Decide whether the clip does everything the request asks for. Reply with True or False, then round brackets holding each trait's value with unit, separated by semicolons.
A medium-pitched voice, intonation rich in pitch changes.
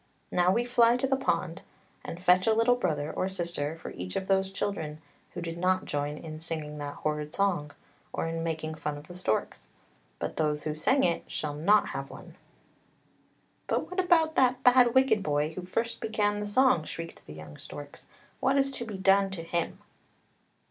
True (180 Hz; 6.2 semitones)